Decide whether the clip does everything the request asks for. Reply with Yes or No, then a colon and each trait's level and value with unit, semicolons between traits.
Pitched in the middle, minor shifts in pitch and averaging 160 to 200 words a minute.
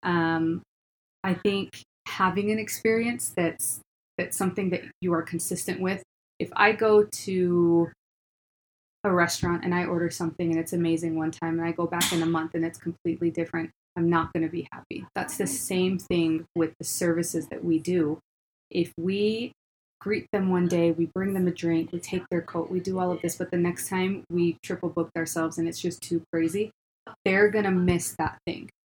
Yes: medium, 175 Hz; narrow, 2.0 semitones; average, 195 wpm